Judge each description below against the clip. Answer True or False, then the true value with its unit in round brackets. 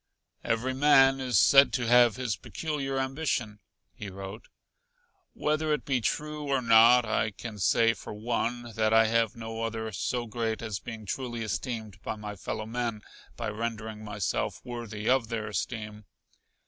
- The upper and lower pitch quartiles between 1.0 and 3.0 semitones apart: True (2.7 semitones)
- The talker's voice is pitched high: False (115 Hz)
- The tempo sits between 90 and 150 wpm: False (160 wpm)